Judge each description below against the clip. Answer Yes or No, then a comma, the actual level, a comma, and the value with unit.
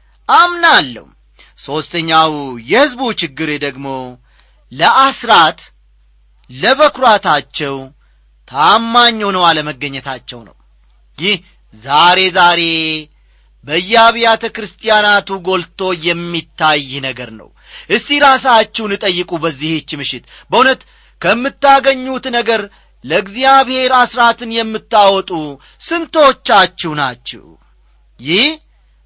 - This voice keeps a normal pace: No, slow, 70 wpm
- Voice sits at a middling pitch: Yes, medium, 180 Hz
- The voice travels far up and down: Yes, wide, 8.4 semitones